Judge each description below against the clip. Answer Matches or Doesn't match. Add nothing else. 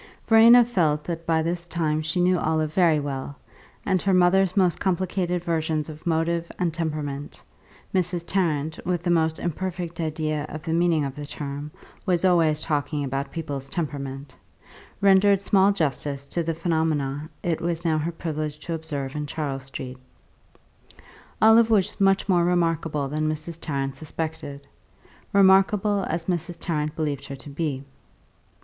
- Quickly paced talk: Doesn't match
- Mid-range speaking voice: Matches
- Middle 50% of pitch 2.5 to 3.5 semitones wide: Matches